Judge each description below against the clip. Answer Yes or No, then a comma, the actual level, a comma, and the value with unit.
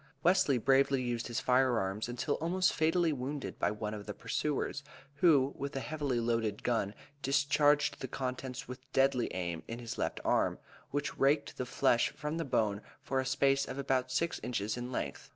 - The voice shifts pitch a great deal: No, average, 3.2 semitones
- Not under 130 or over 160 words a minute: No, average, 185 wpm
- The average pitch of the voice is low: Yes, low, 130 Hz